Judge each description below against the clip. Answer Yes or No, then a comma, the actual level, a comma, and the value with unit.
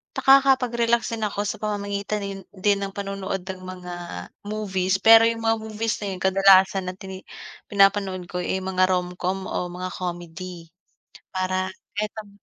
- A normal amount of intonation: No, narrow, 2.3 semitones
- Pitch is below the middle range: No, high, 195 Hz